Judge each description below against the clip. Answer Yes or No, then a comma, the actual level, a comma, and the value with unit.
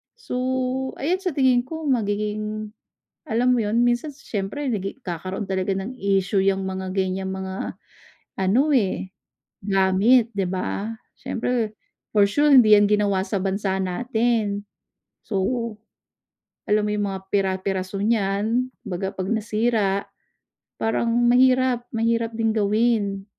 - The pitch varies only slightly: No, average, 3.6 semitones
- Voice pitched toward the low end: No, high, 210 Hz